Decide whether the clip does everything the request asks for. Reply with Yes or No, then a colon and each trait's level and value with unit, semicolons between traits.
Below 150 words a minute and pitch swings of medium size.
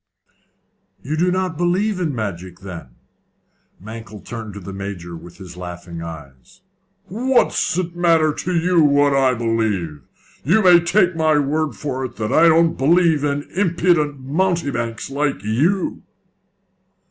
No: average, 140 wpm; wide, 8.8 semitones